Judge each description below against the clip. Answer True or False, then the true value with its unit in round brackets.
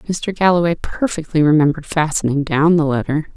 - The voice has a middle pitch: True (160 Hz)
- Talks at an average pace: True (145 wpm)